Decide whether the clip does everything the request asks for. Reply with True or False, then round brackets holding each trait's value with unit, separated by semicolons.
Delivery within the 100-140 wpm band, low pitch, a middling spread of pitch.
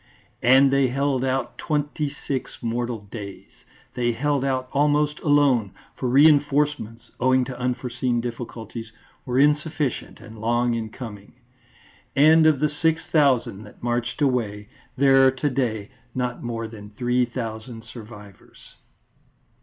True (135 wpm; 125 Hz; 3.3 semitones)